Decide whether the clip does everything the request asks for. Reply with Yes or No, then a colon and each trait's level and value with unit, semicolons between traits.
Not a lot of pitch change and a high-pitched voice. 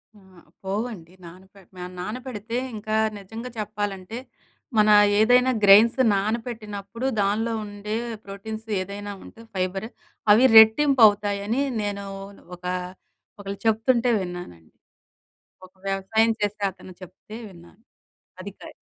Yes: narrow, 2.3 semitones; high, 210 Hz